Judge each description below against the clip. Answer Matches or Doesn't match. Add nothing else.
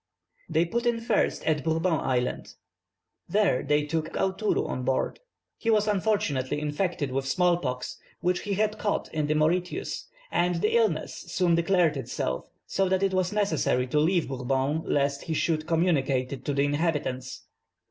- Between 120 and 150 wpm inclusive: Doesn't match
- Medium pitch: Matches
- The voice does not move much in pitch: Doesn't match